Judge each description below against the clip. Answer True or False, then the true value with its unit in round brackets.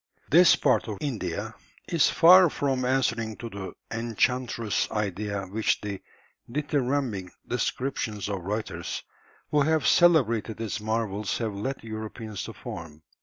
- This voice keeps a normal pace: False (130 wpm)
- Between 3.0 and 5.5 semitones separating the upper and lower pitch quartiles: True (4.3 semitones)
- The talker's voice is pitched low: True (115 Hz)